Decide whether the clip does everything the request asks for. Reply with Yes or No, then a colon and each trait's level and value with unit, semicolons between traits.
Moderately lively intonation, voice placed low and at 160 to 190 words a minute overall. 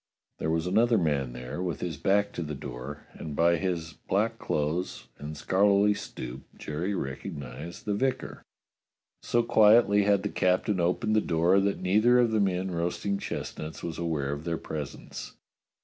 Yes: average, 4.8 semitones; very low, 90 Hz; average, 165 wpm